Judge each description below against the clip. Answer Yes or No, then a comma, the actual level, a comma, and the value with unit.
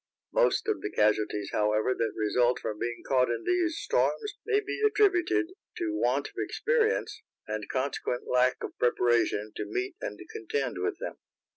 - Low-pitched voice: Yes, low, 125 Hz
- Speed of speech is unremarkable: Yes, average, 160 wpm